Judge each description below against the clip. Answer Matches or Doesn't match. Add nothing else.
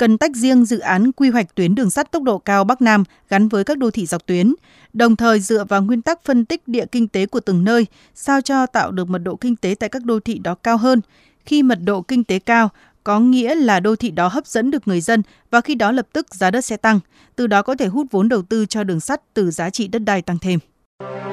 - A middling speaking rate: Doesn't match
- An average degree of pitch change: Matches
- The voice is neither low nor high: Doesn't match